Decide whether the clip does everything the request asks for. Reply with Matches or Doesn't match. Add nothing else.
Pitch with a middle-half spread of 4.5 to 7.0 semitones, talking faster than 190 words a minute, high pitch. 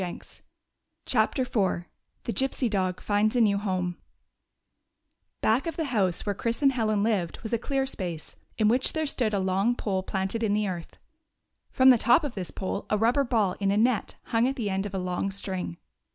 Doesn't match